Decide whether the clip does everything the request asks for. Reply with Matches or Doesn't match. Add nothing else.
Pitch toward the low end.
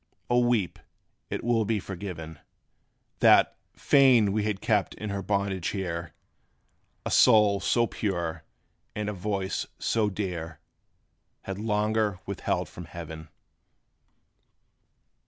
Matches